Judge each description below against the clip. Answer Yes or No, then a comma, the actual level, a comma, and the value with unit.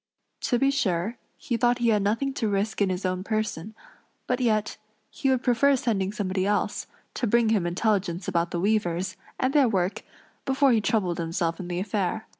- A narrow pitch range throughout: No, average, 4.4 semitones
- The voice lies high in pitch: Yes, high, 210 Hz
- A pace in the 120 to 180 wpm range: No, average, 190 wpm